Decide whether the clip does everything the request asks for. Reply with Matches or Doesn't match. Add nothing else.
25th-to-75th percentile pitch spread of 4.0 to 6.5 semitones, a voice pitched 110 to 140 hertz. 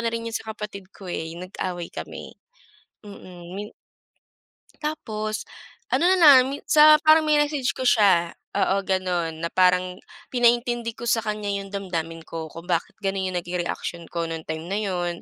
Doesn't match